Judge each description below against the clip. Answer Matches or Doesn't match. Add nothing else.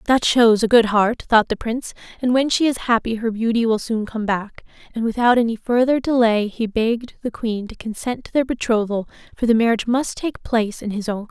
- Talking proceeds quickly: Matches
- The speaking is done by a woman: Matches